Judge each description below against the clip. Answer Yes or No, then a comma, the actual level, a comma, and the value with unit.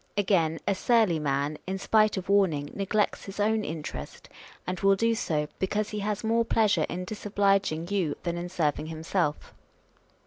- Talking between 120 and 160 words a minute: No, average, 170 wpm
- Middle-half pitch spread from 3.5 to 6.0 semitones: Yes, average, 4.4 semitones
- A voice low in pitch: No, high, 190 Hz